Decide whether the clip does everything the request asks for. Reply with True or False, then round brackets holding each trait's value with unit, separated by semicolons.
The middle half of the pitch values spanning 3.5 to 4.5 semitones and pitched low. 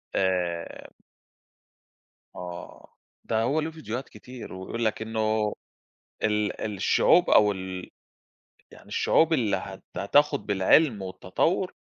False (5.3 semitones; 105 Hz)